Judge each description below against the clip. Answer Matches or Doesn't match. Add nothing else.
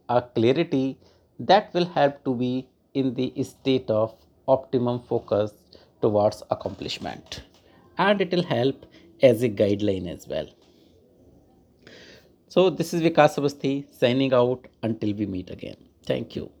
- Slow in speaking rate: Matches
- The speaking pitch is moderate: Doesn't match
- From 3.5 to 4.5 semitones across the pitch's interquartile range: Doesn't match